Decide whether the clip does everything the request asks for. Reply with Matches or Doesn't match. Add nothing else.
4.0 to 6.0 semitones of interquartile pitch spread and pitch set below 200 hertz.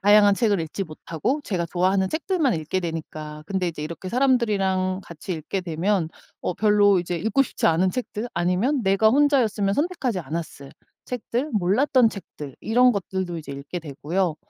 Matches